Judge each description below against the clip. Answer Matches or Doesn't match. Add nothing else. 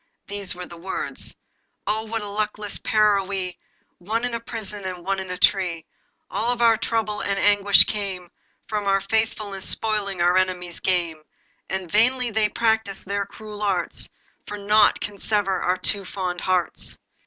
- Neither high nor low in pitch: Doesn't match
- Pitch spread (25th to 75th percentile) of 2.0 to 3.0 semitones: Matches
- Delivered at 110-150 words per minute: Doesn't match